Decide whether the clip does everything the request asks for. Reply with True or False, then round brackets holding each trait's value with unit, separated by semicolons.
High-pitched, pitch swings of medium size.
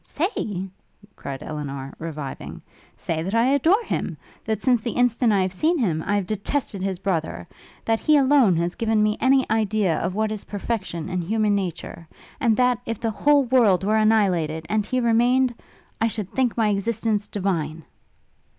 True (215 Hz; 4.5 semitones)